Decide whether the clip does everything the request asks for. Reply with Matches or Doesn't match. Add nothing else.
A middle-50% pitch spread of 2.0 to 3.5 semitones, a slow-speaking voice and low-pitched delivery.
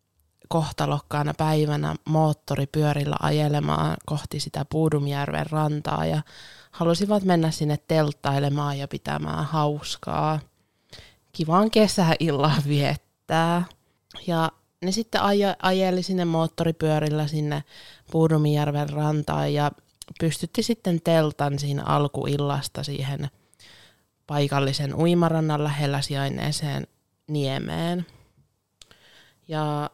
Doesn't match